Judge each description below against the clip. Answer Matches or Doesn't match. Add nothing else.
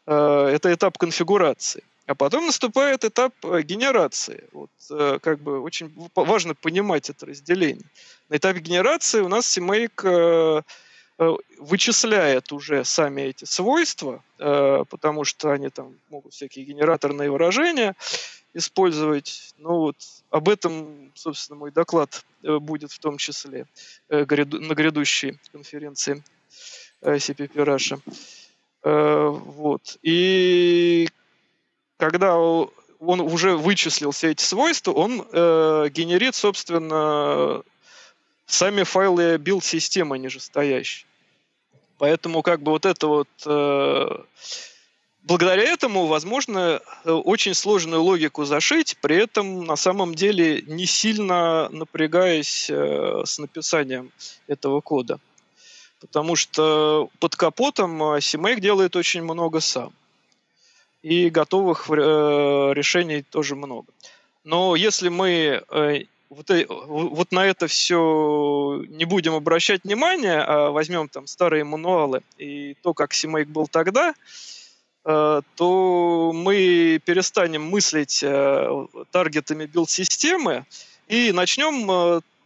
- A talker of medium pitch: Matches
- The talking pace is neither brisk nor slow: Doesn't match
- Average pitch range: Matches